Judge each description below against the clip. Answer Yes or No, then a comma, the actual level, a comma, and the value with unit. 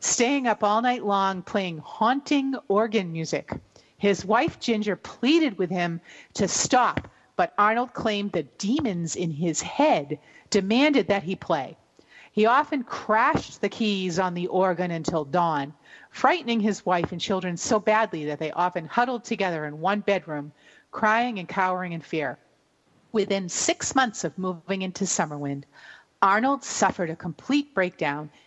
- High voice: Yes, high, 195 Hz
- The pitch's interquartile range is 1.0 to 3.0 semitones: No, average, 4.2 semitones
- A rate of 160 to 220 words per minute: No, average, 150 wpm